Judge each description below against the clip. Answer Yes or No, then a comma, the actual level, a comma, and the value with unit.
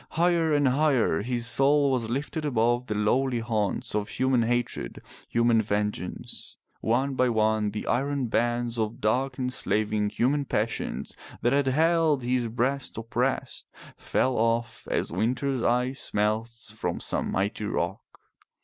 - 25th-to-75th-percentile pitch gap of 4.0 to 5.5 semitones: No, average, 3.4 semitones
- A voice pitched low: Yes, low, 120 Hz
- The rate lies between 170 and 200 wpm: No, average, 140 wpm